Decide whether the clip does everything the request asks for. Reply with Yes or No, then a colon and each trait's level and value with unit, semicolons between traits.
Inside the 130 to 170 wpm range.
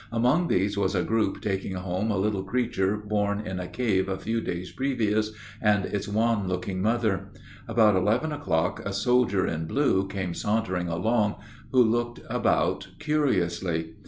Yes: average, 160 wpm